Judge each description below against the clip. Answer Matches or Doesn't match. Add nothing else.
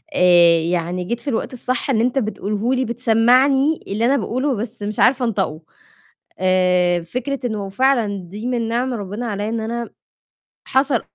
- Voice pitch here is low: Doesn't match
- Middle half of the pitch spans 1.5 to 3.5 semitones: Doesn't match